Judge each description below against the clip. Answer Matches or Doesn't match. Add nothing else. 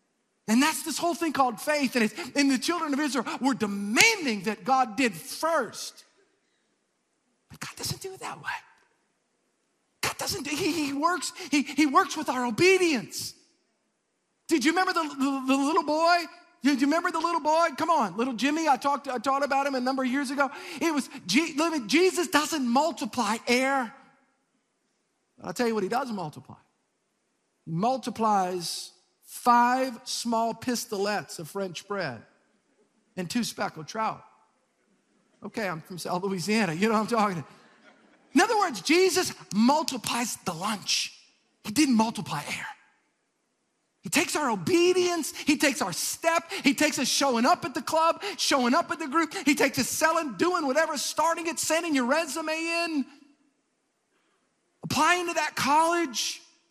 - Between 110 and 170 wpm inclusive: Matches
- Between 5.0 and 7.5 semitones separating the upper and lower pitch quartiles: Matches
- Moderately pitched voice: Doesn't match